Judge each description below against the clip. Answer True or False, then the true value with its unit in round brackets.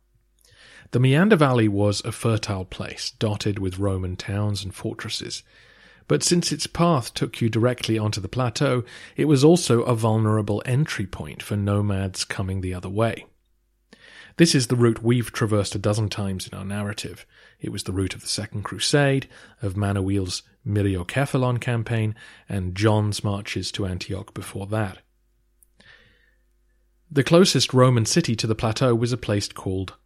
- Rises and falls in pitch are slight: False (3.7 semitones)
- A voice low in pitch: True (110 Hz)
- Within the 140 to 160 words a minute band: True (155 wpm)